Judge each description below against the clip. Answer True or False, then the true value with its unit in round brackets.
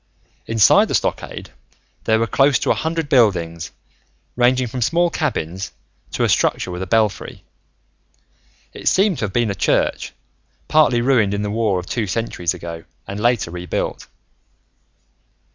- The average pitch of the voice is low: True (110 Hz)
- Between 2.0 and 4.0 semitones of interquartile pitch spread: False (5.3 semitones)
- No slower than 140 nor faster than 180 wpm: True (150 wpm)